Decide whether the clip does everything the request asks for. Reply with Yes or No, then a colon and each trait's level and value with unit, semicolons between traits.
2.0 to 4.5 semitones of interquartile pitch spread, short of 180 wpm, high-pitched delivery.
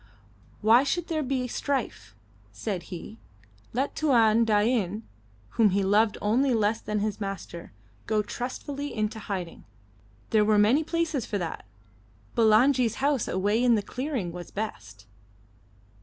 Yes: average, 3.8 semitones; slow, 135 wpm; high, 220 Hz